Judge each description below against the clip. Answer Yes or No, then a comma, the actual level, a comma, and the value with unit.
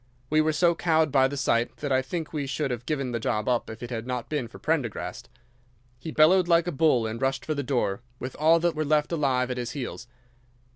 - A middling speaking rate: No, fast, 240 wpm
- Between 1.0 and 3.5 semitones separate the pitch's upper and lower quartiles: No, average, 4.0 semitones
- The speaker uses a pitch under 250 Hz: Yes, medium, 140 Hz